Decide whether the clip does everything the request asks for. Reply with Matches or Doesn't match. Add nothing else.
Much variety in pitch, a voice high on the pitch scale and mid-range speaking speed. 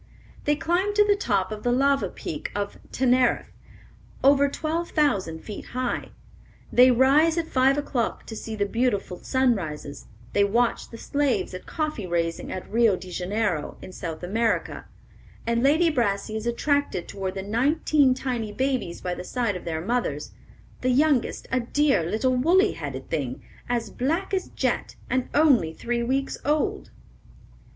Matches